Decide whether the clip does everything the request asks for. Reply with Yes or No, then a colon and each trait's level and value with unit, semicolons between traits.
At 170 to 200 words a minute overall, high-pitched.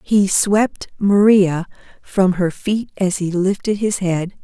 No: average, 150 wpm; high, 195 Hz